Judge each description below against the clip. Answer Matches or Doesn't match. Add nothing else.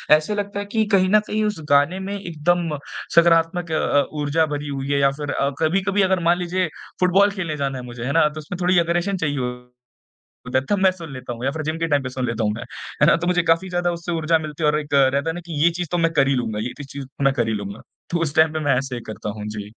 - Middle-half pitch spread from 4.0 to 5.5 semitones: Matches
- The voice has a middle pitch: Matches